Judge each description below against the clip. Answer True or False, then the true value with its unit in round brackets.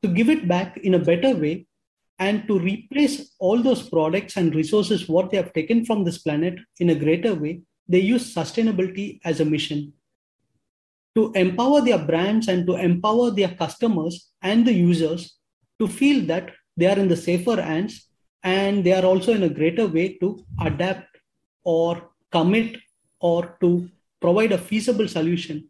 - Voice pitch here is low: False (185 Hz)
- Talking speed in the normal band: True (170 wpm)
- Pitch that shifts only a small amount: False (4.2 semitones)